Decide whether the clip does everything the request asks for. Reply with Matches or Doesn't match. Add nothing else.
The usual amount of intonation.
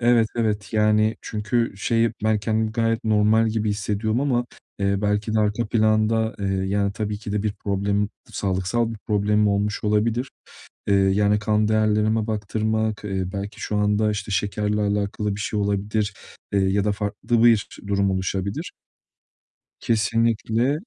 Doesn't match